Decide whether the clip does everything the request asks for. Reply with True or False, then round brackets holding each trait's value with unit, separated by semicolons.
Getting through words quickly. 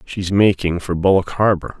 False (165 wpm)